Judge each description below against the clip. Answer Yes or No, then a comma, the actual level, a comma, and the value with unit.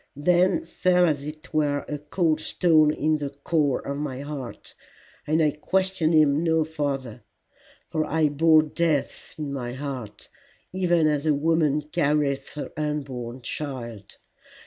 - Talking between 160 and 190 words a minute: No, average, 145 wpm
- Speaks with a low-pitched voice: No, medium, 150 Hz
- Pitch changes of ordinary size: No, narrow, 2.3 semitones